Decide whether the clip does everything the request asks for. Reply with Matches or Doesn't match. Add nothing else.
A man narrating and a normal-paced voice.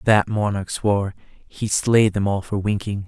Matches